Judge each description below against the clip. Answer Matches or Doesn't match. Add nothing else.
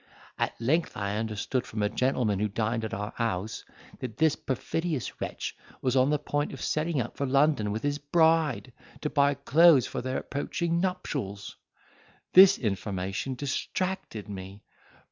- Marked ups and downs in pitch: Matches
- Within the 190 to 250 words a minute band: Doesn't match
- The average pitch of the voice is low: Matches